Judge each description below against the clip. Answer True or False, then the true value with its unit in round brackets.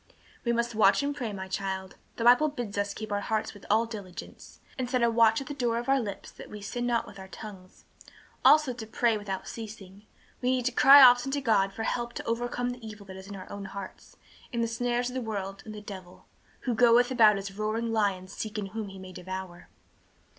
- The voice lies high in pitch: True (220 Hz)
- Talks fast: True (230 wpm)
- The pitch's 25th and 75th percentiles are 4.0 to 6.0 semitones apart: False (3.5 semitones)